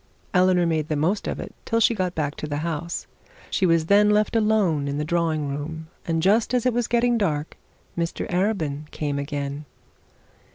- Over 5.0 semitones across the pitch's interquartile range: Yes, wide, 5.4 semitones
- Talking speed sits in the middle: Yes, average, 190 wpm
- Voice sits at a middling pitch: Yes, medium, 165 Hz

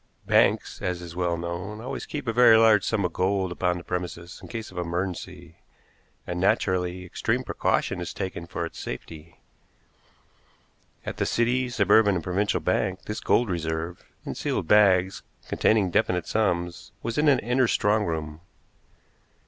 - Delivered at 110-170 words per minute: Yes, average, 155 wpm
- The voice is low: Yes, very low, 90 Hz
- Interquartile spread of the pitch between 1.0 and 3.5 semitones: No, average, 3.9 semitones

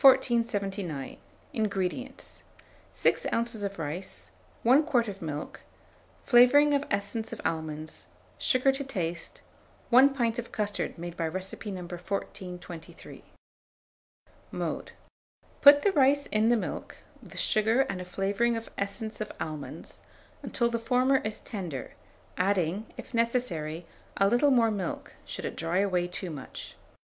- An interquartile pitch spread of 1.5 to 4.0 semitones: No, average, 5.1 semitones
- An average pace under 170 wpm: Yes, slow, 135 wpm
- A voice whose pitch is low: No, high, 205 Hz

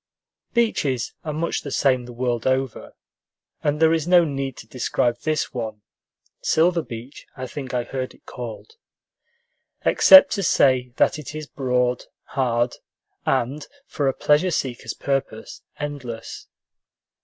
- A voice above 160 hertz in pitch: No, low, 135 Hz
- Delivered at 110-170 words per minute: Yes, average, 140 wpm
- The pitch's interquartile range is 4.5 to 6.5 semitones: No, average, 3.6 semitones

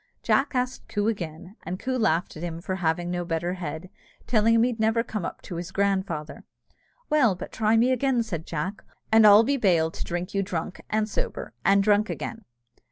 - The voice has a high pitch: Yes, high, 195 Hz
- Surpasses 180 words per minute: Yes, average, 200 wpm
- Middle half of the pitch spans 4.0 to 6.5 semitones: Yes, average, 4.4 semitones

